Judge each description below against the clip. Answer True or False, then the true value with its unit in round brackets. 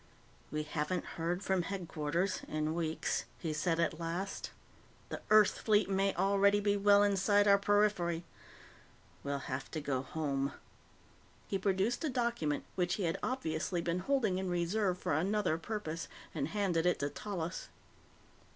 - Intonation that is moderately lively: True (4.0 semitones)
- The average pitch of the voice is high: False (180 Hz)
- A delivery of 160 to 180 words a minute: False (150 wpm)